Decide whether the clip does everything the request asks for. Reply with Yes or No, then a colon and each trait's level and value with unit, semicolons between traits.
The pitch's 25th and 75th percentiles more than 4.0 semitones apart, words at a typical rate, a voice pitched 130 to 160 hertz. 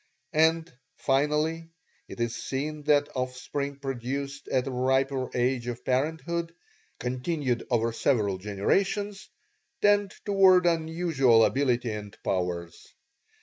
No: average, 4.7 semitones; slow, 105 wpm; low, 135 Hz